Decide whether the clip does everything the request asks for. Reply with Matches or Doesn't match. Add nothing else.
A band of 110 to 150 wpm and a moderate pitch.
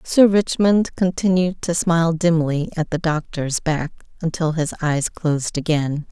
Matches